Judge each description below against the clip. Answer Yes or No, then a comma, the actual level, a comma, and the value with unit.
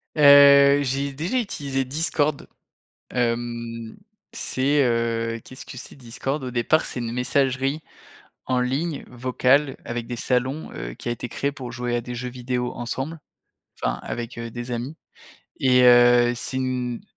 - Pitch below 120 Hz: No, low, 125 Hz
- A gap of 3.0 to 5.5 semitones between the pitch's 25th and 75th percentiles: No, narrow, 2.6 semitones